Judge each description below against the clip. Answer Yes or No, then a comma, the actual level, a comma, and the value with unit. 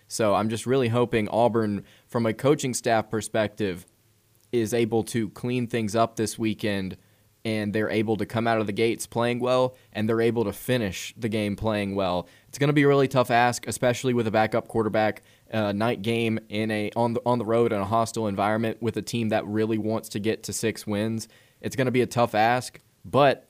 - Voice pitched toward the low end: Yes, low, 110 Hz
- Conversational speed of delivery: No, fast, 215 wpm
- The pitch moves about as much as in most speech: No, narrow, 1.9 semitones